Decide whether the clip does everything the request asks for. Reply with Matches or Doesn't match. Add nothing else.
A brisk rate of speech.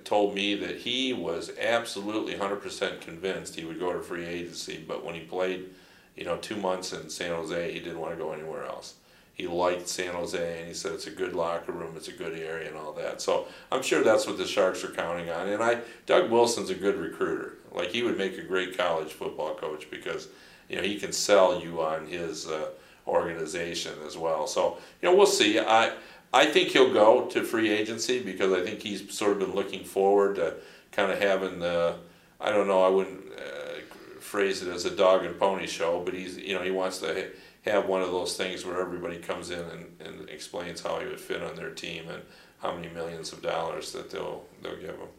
Matches